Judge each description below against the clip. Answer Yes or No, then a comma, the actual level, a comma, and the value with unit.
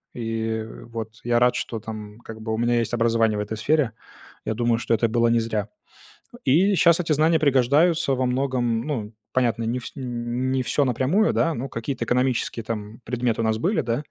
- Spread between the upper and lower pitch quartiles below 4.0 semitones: Yes, average, 2.9 semitones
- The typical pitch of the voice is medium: No, low, 120 Hz